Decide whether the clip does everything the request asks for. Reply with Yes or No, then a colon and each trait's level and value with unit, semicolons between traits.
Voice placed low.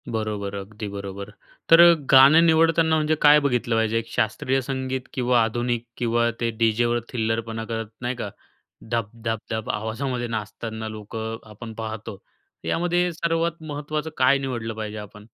Yes: low, 115 Hz